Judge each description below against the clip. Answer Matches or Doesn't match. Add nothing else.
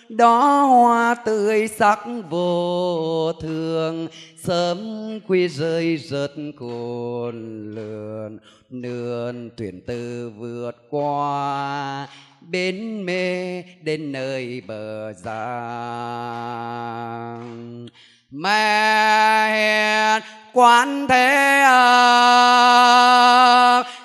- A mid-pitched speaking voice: Matches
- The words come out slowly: Matches